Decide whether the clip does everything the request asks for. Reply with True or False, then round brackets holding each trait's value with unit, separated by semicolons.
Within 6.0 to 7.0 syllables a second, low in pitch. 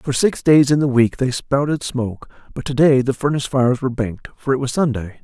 True (6.1 syllables/s; 130 Hz)